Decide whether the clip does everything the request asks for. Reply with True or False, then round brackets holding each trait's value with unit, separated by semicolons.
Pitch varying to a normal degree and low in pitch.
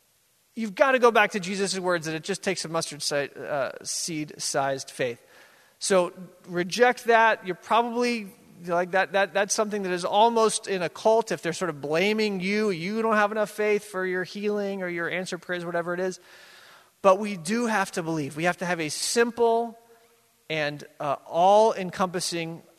False (3.7 semitones; 190 Hz)